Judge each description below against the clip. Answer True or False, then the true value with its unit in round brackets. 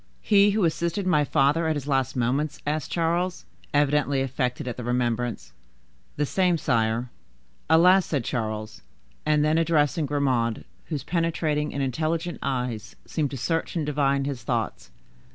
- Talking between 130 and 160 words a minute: True (150 wpm)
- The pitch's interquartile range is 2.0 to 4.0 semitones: False (4.5 semitones)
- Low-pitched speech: False (145 Hz)